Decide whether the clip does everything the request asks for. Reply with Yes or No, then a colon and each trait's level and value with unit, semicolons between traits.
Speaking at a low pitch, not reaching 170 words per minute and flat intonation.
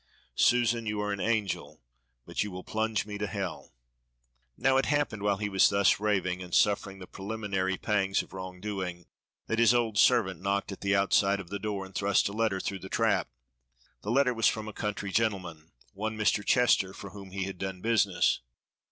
No: low, 100 Hz; average, 195 wpm; narrow, 2.1 semitones